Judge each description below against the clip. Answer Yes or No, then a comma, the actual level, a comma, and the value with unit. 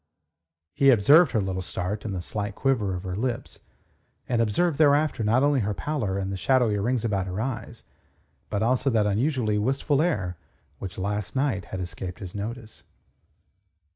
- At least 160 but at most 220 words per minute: Yes, average, 170 wpm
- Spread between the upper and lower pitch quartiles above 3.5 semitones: Yes, average, 5.2 semitones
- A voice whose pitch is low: Yes, low, 110 Hz